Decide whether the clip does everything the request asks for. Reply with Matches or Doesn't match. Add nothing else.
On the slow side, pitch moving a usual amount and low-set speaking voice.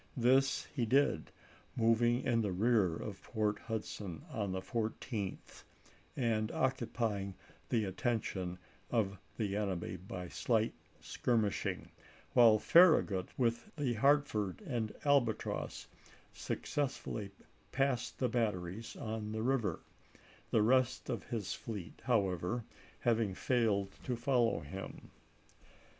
Matches